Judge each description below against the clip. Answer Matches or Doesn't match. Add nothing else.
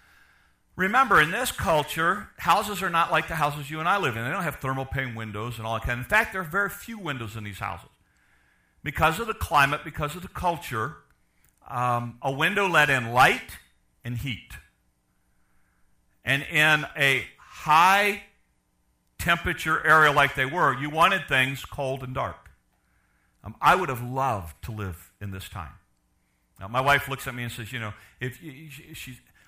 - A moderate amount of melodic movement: Doesn't match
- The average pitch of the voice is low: Matches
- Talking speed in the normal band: Matches